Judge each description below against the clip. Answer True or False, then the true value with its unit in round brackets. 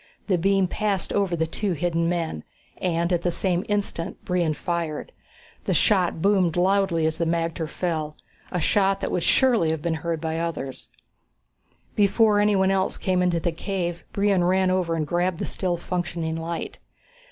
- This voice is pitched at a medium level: True (175 Hz)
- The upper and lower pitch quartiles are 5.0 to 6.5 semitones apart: False (2.5 semitones)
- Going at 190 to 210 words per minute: False (175 wpm)